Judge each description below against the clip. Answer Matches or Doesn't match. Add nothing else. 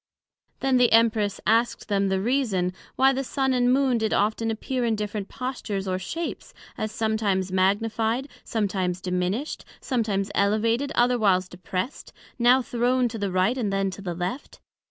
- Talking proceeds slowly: Doesn't match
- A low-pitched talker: Doesn't match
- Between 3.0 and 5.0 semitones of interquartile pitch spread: Matches